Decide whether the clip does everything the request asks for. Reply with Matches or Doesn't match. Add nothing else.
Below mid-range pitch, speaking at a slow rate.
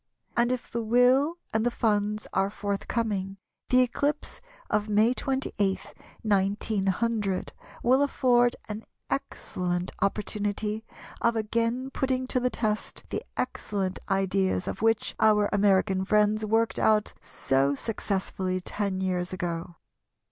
Doesn't match